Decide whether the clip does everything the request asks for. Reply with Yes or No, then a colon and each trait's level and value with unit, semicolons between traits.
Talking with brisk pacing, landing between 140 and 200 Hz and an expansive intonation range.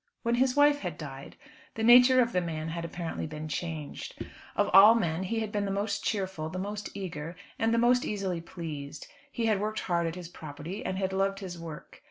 No: fast, 215 wpm; high, 190 Hz; average, 4.7 semitones